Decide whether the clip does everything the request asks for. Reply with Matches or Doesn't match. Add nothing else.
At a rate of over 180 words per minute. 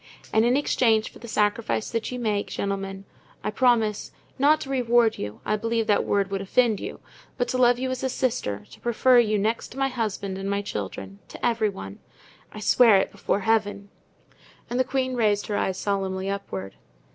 Matches